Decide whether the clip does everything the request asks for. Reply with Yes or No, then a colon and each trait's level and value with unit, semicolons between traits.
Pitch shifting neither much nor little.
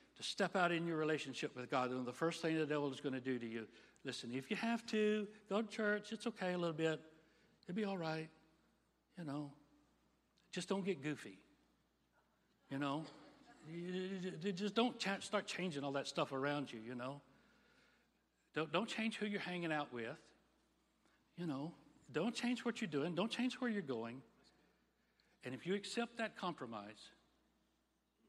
No: wide, 6.7 semitones